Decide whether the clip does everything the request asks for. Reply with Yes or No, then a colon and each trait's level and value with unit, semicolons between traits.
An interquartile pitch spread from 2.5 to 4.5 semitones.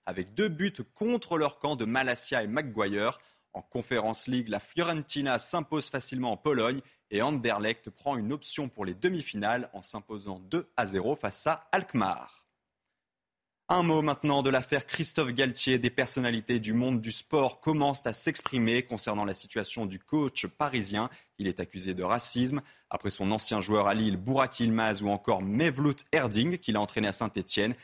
No: average, 5.2 semitones